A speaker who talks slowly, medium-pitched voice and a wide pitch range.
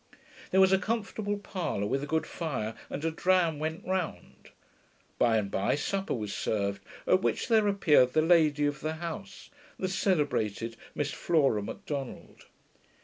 No: average, 155 wpm; medium, 160 Hz; wide, 6.1 semitones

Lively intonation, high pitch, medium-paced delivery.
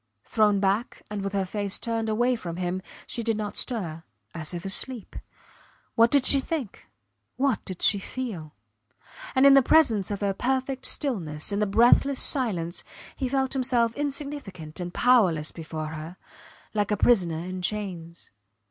Yes: wide, 5.8 semitones; high, 210 Hz; average, 160 wpm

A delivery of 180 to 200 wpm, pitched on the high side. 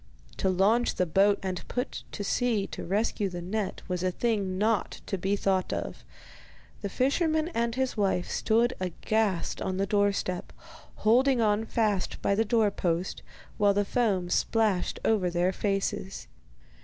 No: average, 155 wpm; high, 200 Hz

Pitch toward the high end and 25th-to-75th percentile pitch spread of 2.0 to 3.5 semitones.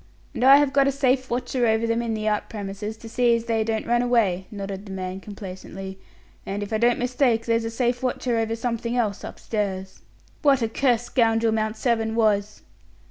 Yes: high, 225 Hz; narrow, 2.6 semitones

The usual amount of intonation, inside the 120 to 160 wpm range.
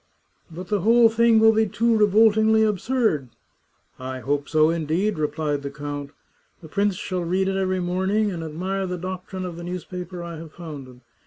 No: average, 4.8 semitones; average, 195 wpm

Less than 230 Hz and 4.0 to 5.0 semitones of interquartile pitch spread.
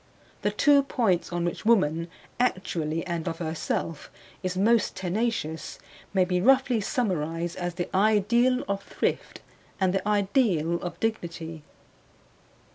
Yes: medium, 185 Hz; average, 4.7 semitones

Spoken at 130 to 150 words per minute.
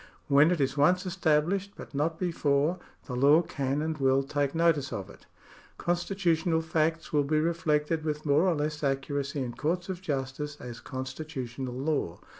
No: average, 165 wpm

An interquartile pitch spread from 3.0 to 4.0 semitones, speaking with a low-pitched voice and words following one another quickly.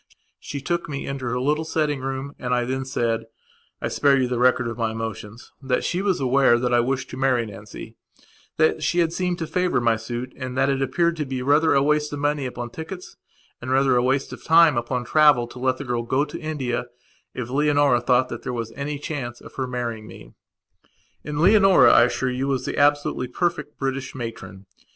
Yes: average, 3.3 semitones; low, 130 Hz; fast, 210 wpm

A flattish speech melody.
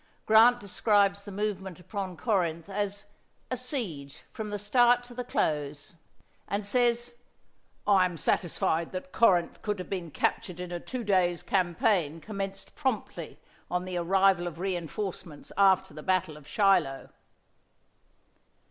No: average, 3.2 semitones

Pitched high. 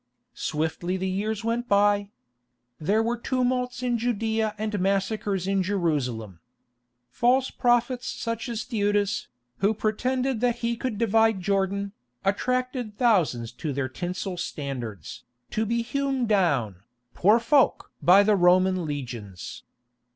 Yes: high, 205 Hz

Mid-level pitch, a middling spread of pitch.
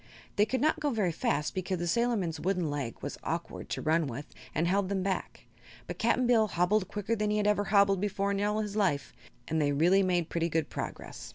No: high, 195 Hz; average, 3.9 semitones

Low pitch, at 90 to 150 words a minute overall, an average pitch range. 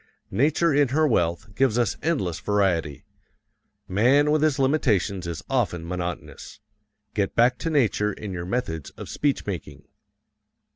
No: low, 105 Hz; average, 140 wpm; wide, 7.6 semitones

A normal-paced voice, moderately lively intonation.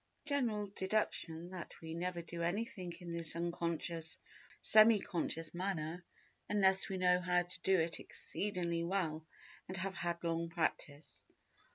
No: average, 145 wpm; narrow, 2.1 semitones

